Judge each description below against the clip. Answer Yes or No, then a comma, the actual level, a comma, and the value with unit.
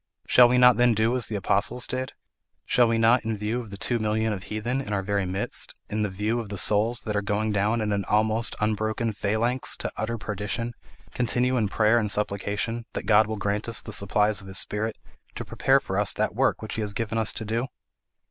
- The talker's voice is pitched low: Yes, low, 110 Hz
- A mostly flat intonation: Yes, narrow, 2.1 semitones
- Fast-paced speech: Yes, fast, 225 wpm